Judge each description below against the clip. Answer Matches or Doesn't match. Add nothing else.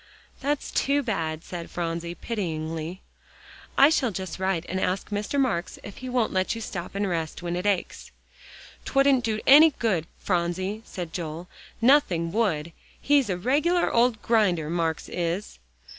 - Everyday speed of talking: Matches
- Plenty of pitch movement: Matches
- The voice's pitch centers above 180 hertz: Matches